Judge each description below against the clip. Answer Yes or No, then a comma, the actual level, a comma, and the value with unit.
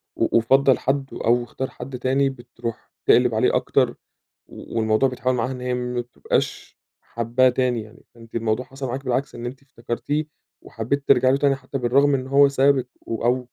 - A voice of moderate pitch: No, low, 125 Hz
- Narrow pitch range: Yes, narrow, 2.2 semitones